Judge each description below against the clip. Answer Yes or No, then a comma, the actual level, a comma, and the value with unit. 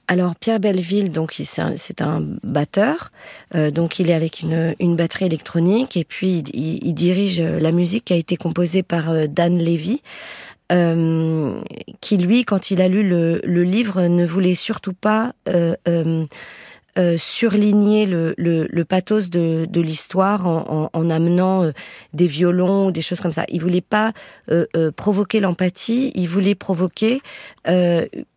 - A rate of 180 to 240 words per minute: No, average, 170 wpm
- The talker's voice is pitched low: No, medium, 180 Hz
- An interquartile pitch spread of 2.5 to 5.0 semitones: Yes, average, 3.1 semitones